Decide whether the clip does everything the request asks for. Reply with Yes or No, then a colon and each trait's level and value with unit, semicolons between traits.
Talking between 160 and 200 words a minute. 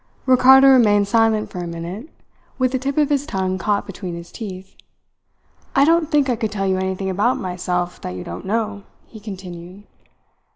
Yes: average, 180 wpm